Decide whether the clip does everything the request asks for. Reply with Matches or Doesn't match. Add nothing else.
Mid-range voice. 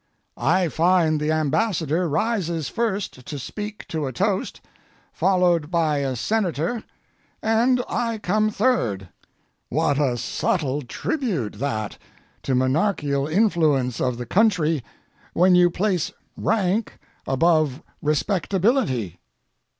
Matches